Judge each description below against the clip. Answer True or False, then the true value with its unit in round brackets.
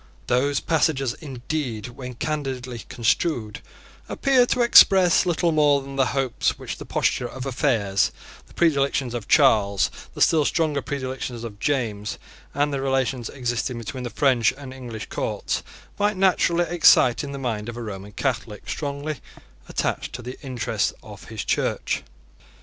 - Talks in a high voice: False (130 Hz)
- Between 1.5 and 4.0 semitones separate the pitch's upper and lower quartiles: True (3.6 semitones)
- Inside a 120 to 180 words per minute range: True (150 wpm)